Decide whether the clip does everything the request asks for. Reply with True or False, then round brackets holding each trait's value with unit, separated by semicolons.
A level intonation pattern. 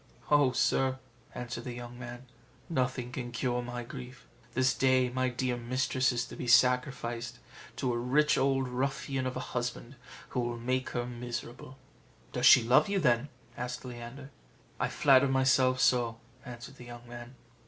True (1.4 semitones)